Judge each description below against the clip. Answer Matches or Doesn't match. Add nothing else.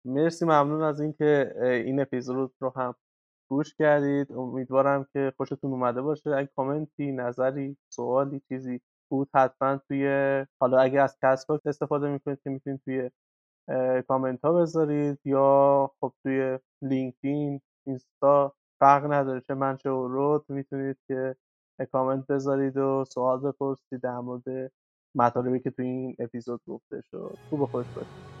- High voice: Doesn't match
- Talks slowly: Doesn't match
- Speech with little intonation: Matches